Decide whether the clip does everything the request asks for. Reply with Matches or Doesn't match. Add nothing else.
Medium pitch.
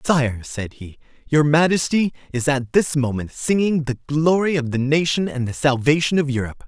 Matches